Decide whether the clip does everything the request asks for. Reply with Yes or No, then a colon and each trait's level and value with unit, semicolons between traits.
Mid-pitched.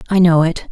Yes: medium, 170 Hz